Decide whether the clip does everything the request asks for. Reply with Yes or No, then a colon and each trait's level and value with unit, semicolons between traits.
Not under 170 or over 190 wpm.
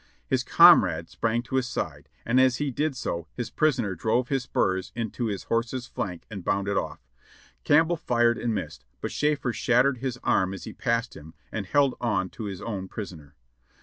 Yes: average, 185 wpm